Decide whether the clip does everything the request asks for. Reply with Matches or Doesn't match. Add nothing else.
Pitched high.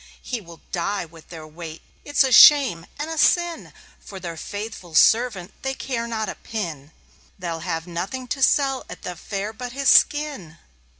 Matches